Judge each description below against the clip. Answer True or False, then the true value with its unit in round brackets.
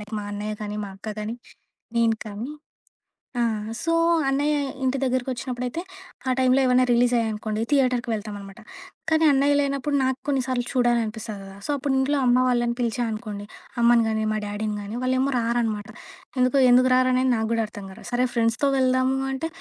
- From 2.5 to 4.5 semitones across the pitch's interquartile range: True (3.0 semitones)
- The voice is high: True (245 Hz)